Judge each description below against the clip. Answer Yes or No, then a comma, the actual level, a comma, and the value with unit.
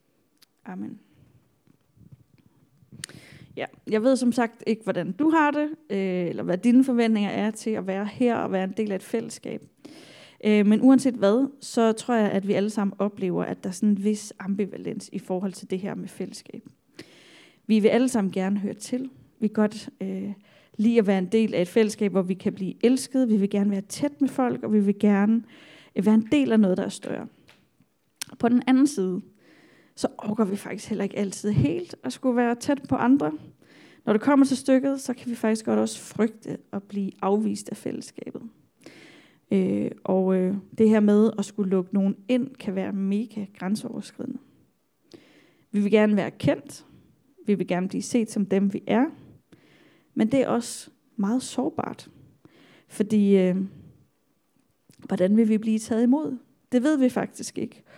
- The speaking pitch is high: Yes, high, 215 Hz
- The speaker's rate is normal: Yes, average, 185 wpm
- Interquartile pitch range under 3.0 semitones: No, average, 3.6 semitones